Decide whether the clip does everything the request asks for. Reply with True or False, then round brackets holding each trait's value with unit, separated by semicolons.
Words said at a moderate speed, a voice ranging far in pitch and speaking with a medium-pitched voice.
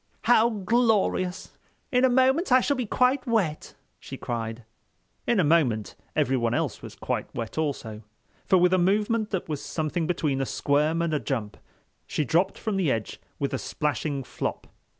True (170 wpm; 8.1 semitones; 165 Hz)